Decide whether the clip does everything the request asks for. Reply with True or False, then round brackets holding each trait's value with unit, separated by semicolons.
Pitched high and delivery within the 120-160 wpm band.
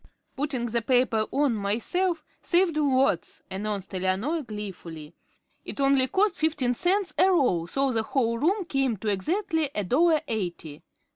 True (255 Hz; 145 wpm)